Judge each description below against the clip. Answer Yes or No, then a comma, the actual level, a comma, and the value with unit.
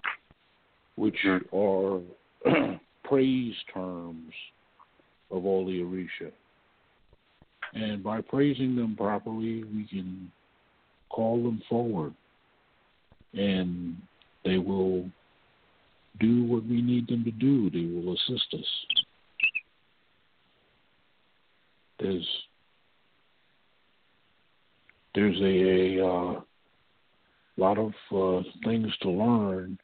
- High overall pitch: No, low, 100 Hz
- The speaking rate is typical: No, slow, 85 wpm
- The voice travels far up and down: No, average, 3.6 semitones